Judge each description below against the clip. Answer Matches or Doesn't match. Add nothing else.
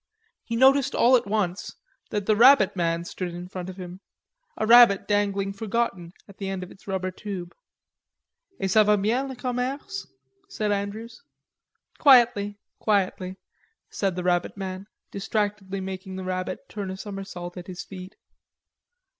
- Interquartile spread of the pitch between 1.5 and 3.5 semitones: Matches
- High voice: Matches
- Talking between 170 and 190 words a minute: Doesn't match